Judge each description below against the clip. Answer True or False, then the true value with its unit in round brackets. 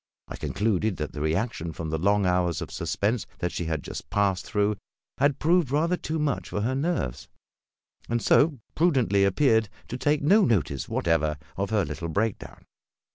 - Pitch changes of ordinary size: False (7.9 semitones)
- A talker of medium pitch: False (105 Hz)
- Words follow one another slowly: False (180 wpm)